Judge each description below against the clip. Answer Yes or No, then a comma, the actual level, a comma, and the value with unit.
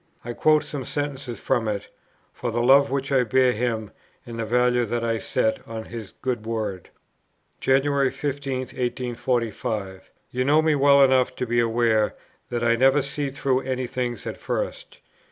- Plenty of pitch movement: No, average, 2.7 semitones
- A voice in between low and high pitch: No, low, 125 Hz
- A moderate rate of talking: Yes, average, 170 wpm